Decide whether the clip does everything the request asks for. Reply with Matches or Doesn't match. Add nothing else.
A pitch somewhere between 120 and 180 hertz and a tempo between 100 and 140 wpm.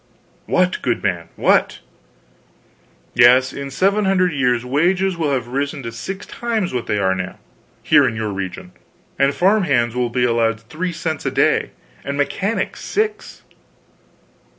Doesn't match